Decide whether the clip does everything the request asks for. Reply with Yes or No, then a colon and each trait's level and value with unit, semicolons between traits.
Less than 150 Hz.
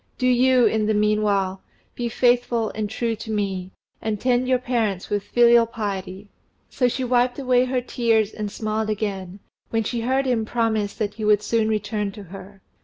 No: high, 220 Hz